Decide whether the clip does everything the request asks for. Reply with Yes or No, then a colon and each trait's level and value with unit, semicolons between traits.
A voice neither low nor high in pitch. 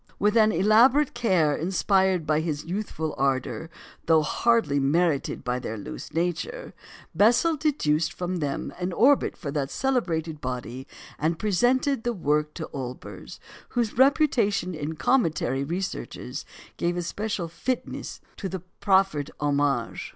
Yes: medium, 175 Hz